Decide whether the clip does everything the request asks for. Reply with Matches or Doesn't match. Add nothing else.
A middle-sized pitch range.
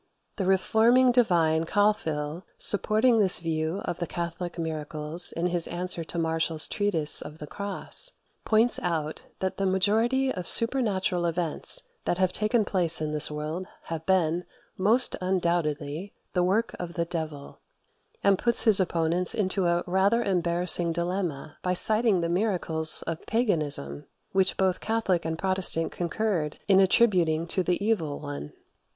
Matches